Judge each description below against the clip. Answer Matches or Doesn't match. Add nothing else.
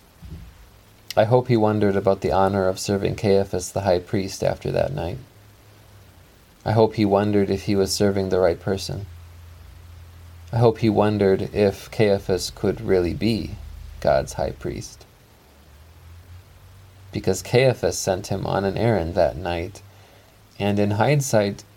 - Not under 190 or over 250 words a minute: Doesn't match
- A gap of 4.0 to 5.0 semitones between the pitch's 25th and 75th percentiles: Doesn't match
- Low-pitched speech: Matches